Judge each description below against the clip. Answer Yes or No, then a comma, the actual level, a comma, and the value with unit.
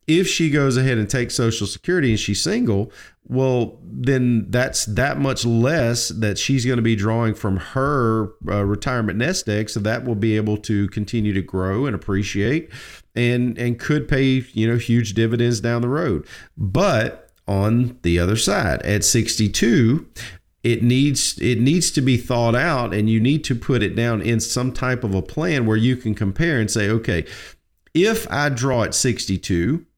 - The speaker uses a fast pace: No, average, 180 wpm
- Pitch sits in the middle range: No, low, 115 Hz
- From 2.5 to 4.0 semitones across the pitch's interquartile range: Yes, average, 3.5 semitones